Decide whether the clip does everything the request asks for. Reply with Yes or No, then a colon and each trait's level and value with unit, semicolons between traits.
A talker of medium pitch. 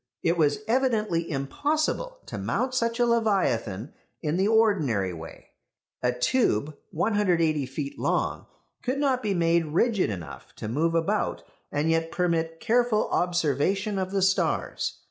Yes: medium, 175 Hz